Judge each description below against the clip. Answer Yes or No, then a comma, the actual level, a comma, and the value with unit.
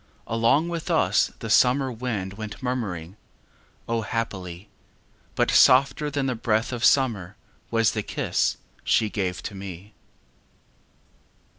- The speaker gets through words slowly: Yes, slow, 120 wpm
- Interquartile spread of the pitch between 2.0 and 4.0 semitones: No, average, 4.5 semitones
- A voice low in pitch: Yes, low, 115 Hz